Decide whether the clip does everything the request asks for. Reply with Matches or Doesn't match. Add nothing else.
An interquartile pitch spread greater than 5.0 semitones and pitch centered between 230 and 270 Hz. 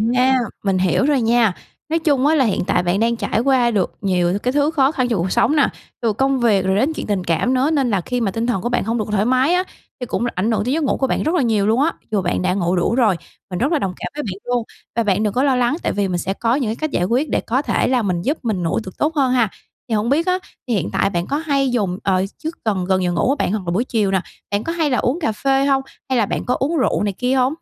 Matches